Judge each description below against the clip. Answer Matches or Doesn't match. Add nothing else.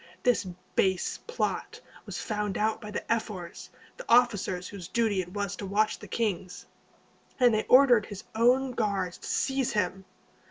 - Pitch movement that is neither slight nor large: Matches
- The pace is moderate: Matches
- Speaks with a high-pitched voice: Matches